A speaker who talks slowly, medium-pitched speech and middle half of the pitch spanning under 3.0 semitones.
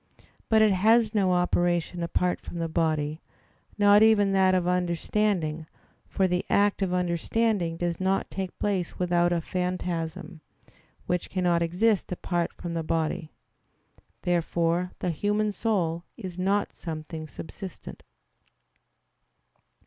Yes: slow, 125 wpm; medium, 180 Hz; narrow, 2.5 semitones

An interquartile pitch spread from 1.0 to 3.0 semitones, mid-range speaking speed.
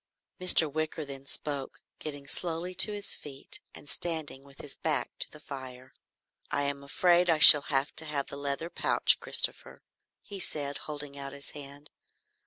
Yes: narrow, 2.4 semitones; average, 170 wpm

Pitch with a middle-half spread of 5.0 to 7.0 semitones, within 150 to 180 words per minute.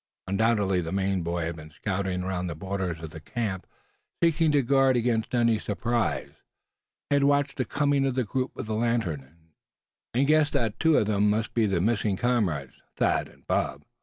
No: wide, 5.4 semitones; average, 190 wpm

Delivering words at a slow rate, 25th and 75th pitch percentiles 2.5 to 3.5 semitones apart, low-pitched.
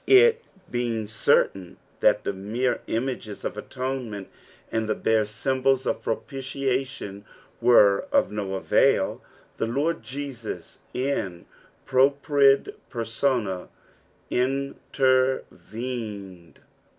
No: slow, 90 wpm; average, 4.1 semitones; low, 125 Hz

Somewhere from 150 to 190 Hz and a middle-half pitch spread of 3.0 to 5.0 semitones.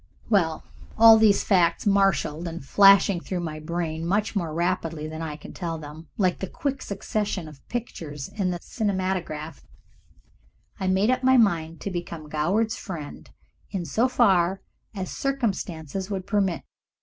Yes: medium, 185 Hz; average, 3.9 semitones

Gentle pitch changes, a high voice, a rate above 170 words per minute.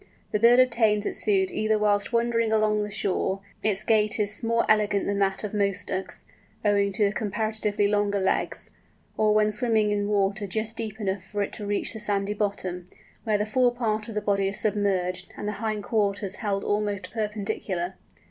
Yes: narrow, 1.4 semitones; high, 210 Hz; average, 185 wpm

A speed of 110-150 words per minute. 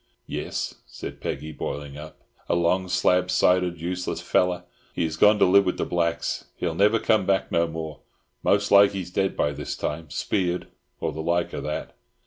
No: average, 180 wpm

